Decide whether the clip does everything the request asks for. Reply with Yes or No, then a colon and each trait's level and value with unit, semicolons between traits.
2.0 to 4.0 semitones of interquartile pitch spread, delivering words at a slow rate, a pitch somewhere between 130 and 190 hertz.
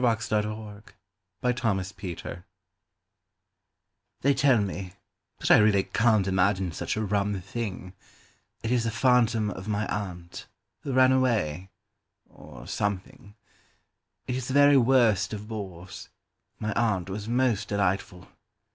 No: average, 3.7 semitones; slow, 110 wpm; low, 105 Hz